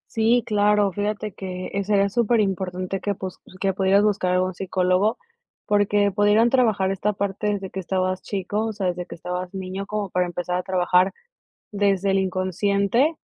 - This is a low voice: No, high, 195 Hz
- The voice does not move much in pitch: Yes, narrow, 1.9 semitones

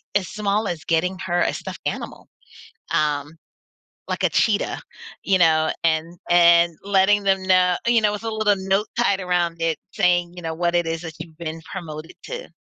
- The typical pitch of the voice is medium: Yes, medium, 175 Hz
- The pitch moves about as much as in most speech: Yes, average, 3.2 semitones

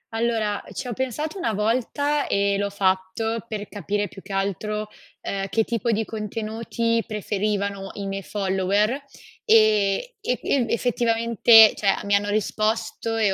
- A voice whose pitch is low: No, high, 215 Hz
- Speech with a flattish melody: Yes, narrow, 2.3 semitones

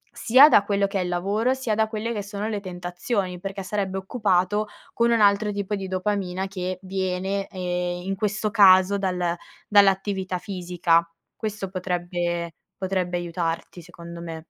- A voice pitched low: No, high, 190 Hz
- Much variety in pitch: No, narrow, 2.4 semitones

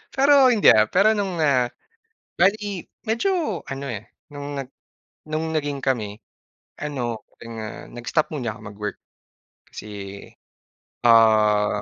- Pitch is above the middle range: No, low, 135 Hz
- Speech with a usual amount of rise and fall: No, wide, 7.6 semitones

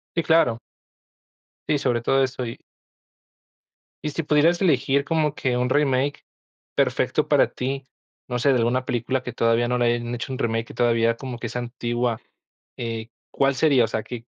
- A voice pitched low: Yes, low, 125 Hz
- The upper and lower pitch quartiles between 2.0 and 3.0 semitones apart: Yes, average, 2.7 semitones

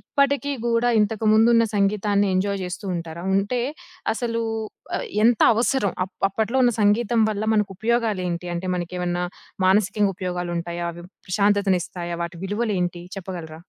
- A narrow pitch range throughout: No, average, 3.9 semitones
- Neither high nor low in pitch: No, high, 200 Hz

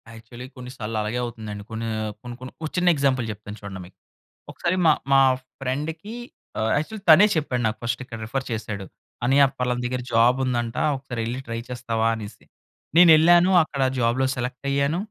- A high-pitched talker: No, low, 125 Hz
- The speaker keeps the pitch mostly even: No, average, 3.6 semitones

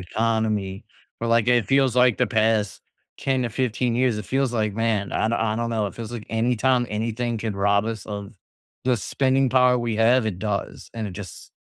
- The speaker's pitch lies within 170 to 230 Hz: No, low, 115 Hz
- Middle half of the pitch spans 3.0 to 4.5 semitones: No, narrow, 2.6 semitones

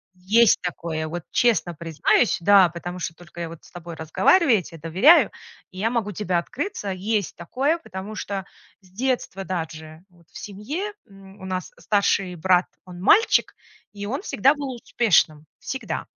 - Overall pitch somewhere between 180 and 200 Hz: Yes, high, 190 Hz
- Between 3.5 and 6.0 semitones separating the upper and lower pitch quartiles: Yes, average, 4.7 semitones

